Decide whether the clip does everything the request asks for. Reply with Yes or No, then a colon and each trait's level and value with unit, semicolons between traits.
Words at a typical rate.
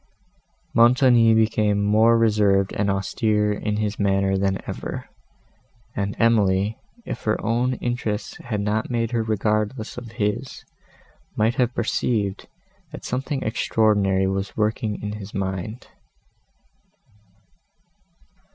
No: slow, 115 wpm